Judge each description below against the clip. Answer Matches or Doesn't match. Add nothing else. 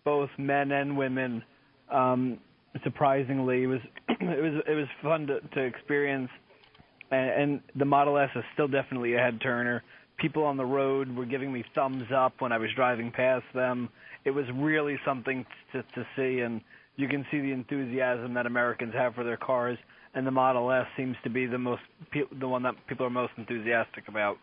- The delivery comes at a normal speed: Matches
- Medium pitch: Doesn't match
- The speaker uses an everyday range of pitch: Doesn't match